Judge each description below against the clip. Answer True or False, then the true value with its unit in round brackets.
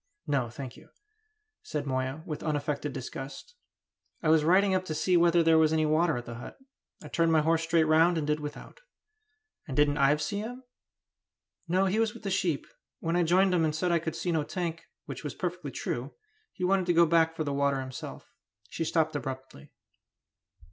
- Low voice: False (160 Hz)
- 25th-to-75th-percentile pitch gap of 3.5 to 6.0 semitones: False (3.0 semitones)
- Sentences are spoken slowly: False (200 wpm)